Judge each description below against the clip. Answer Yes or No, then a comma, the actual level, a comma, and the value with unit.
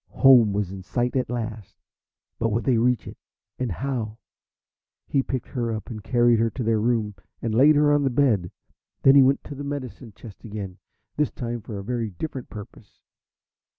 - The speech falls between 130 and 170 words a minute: No, average, 190 wpm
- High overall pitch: No, low, 120 Hz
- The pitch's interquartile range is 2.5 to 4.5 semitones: Yes, average, 3.5 semitones